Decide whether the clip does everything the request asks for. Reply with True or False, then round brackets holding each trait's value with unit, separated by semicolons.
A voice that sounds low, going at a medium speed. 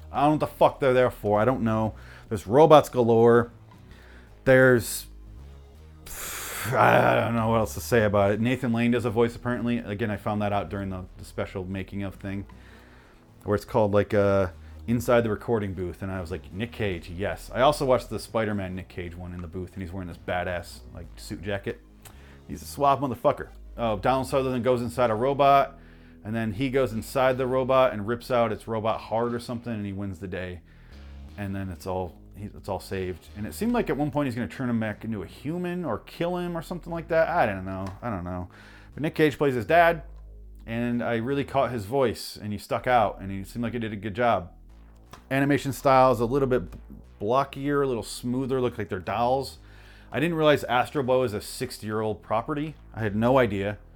False (110 Hz; 220 wpm)